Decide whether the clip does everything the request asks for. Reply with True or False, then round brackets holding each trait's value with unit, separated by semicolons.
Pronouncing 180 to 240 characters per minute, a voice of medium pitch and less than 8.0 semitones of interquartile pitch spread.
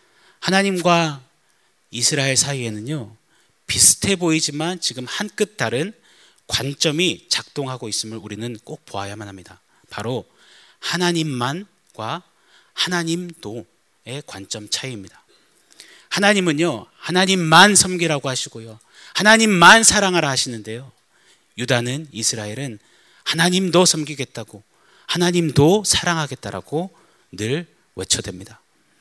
False (270 characters per minute; 150 Hz; 7.3 semitones)